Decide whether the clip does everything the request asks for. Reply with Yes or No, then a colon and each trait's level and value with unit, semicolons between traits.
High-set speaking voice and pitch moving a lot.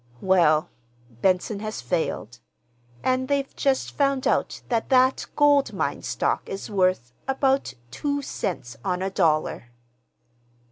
Yes: high, 205 Hz; wide, 7.2 semitones